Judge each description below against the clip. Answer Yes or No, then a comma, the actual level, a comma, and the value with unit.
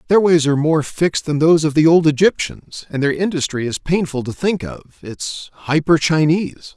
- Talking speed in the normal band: Yes, average, 195 wpm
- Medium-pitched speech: Yes, medium, 155 Hz